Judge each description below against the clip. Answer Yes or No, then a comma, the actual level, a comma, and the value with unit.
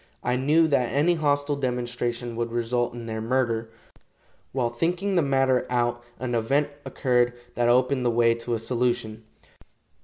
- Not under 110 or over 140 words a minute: No, average, 155 wpm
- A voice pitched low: Yes, low, 125 Hz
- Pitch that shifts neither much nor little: No, narrow, 2.3 semitones